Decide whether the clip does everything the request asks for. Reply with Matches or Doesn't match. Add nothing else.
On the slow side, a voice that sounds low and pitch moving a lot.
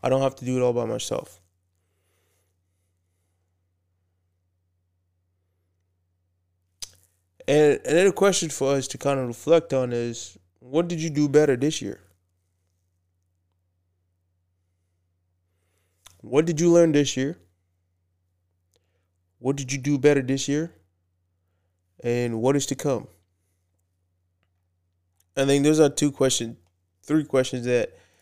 Matches